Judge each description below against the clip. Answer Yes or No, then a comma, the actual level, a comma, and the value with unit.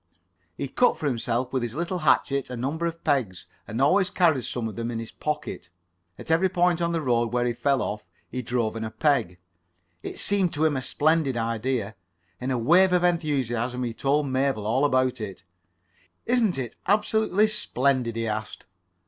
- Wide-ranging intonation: Yes, wide, 5.8 semitones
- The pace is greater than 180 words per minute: Yes, average, 190 wpm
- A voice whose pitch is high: No, low, 130 Hz